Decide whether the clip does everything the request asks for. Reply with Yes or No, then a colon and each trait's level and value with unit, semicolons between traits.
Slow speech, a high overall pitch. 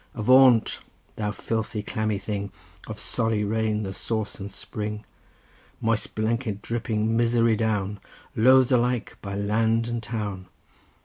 No: slow, 125 wpm; low, 110 Hz